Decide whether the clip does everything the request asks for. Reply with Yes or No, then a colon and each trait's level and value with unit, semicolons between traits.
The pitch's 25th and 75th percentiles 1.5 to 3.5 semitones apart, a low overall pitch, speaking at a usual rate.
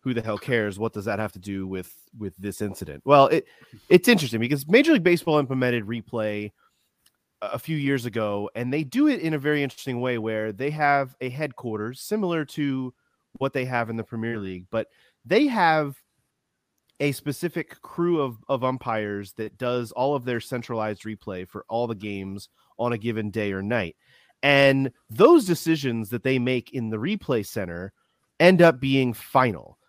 No: average, 4.7 semitones; low, 120 Hz; average, 185 wpm